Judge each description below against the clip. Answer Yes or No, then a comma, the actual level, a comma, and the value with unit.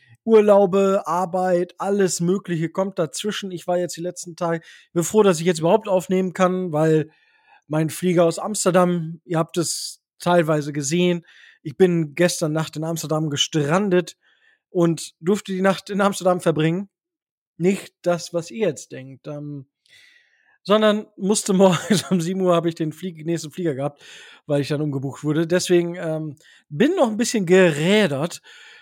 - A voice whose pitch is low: No, medium, 175 Hz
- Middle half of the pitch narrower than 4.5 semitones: Yes, average, 3.1 semitones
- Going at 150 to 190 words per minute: Yes, average, 160 wpm